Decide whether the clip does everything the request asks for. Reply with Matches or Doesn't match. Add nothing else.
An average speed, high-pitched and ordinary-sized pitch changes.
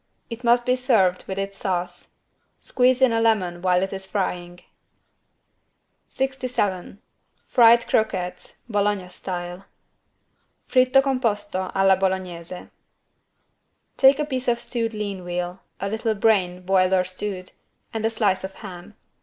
Doesn't match